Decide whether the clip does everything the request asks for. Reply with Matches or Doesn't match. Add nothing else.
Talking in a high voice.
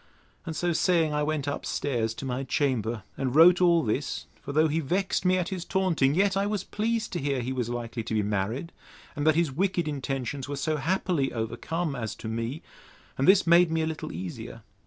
Doesn't match